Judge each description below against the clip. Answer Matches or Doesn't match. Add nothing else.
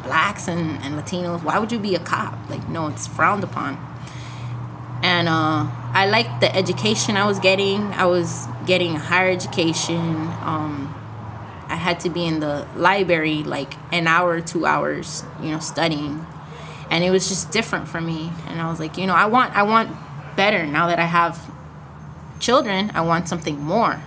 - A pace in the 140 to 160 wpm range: Doesn't match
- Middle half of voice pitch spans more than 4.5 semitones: Doesn't match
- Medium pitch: Matches